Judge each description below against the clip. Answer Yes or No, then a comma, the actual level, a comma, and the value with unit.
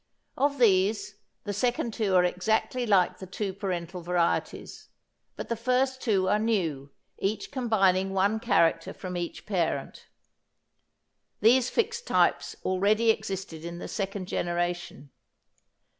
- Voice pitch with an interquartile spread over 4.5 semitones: No, average, 3.8 semitones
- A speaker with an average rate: No, slow, 130 wpm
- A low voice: No, high, 195 Hz